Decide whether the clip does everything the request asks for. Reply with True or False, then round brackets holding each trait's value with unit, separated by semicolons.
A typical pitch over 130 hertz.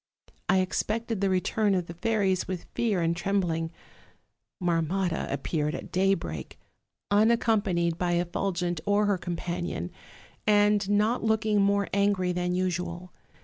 True (185 Hz)